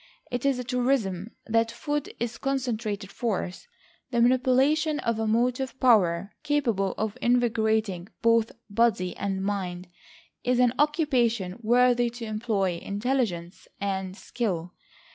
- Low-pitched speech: No, high, 230 Hz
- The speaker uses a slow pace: Yes, slow, 125 wpm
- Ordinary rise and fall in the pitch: Yes, average, 4.0 semitones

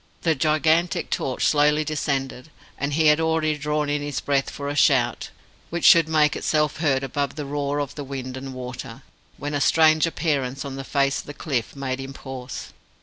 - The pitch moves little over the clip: Yes, narrow, 2.2 semitones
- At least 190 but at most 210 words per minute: Yes, average, 195 wpm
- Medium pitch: Yes, medium, 145 Hz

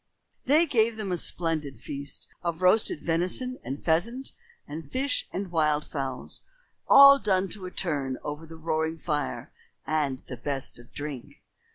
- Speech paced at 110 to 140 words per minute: No, average, 155 wpm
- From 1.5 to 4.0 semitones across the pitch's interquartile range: No, average, 5.0 semitones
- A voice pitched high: No, medium, 165 Hz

